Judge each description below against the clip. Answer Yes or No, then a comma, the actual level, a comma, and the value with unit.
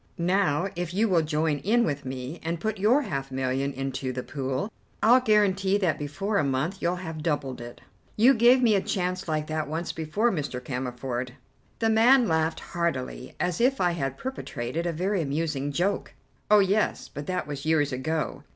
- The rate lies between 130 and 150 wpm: No, average, 185 wpm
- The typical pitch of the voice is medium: Yes, medium, 160 Hz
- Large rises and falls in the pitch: Yes, wide, 6.1 semitones